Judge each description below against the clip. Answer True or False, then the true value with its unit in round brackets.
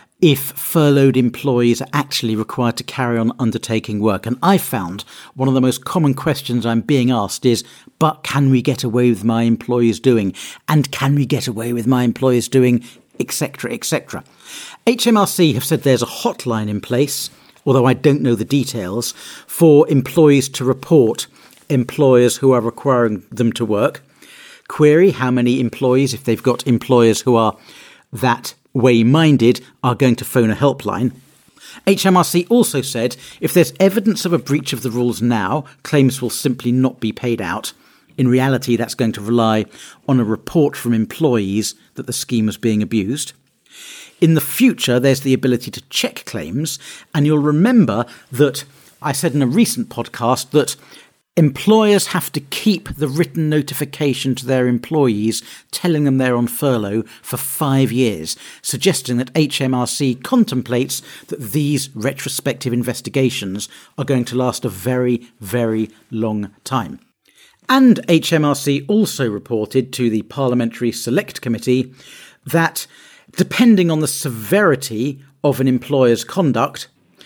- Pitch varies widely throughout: False (3.6 semitones)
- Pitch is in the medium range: False (130 Hz)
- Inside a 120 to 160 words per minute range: True (155 wpm)